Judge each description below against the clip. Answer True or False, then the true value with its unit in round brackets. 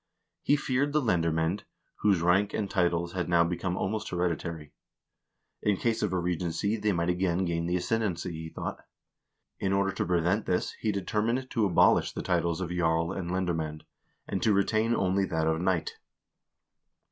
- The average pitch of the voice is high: False (90 Hz)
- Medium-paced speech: True (165 wpm)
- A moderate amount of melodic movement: True (3.3 semitones)